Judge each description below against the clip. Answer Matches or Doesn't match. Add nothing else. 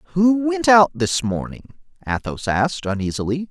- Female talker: Doesn't match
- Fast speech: Doesn't match